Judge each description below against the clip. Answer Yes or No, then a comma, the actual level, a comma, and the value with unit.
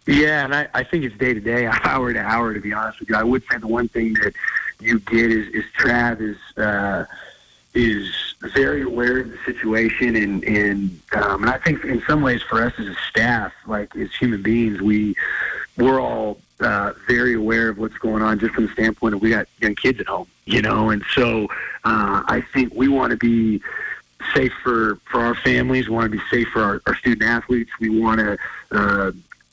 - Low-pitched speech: Yes, low, 115 Hz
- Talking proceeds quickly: Yes, fast, 215 wpm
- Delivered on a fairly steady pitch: Yes, narrow, 2.1 semitones